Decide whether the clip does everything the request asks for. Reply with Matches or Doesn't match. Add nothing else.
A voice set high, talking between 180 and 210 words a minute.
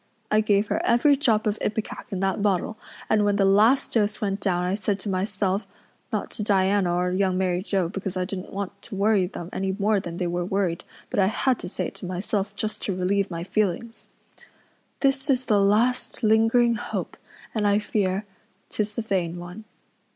Matches